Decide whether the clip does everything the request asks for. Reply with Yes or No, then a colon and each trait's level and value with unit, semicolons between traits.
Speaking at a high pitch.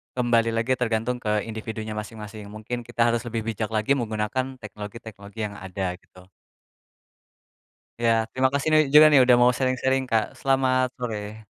No: low, 115 Hz